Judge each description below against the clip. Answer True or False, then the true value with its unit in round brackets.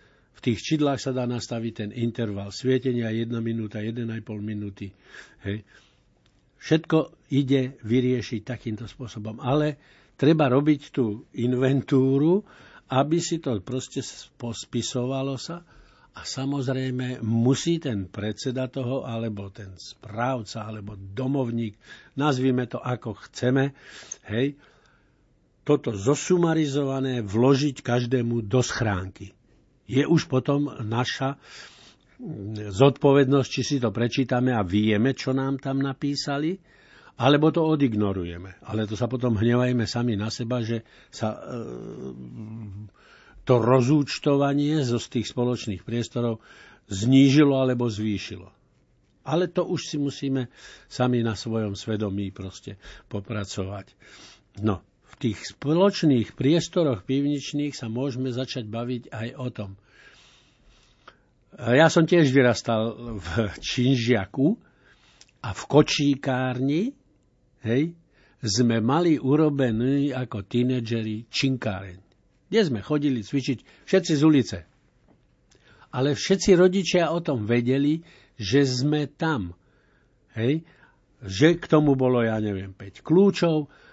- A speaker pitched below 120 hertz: False (125 Hz)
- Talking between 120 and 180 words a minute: False (110 wpm)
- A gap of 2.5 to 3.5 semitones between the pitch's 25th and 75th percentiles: False (4.3 semitones)